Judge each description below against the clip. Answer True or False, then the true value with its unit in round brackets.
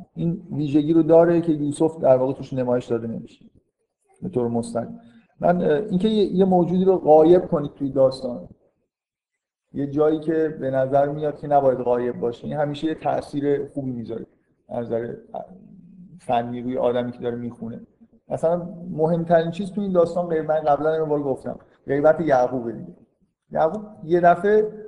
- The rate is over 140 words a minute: True (155 wpm)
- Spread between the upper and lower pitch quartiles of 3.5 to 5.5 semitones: True (5.1 semitones)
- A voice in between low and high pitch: True (155 Hz)